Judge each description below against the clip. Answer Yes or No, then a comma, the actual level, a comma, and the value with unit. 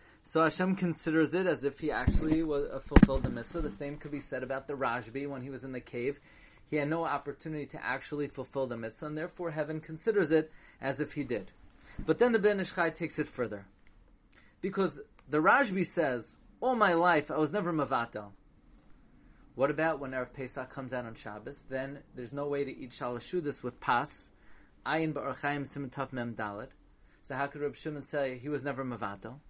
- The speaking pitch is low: No, medium, 145 Hz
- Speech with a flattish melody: No, average, 3.5 semitones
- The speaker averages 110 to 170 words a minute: No, average, 185 wpm